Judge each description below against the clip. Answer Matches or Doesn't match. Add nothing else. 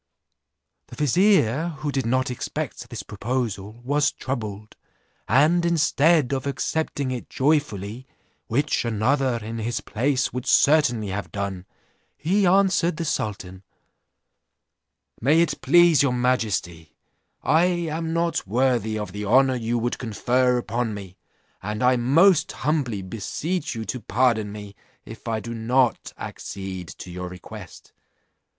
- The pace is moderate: Doesn't match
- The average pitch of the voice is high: Doesn't match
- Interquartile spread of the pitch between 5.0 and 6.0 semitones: Matches